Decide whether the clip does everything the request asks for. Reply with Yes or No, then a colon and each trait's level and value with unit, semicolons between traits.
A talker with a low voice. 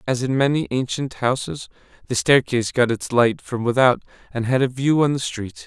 Yes: low, 125 Hz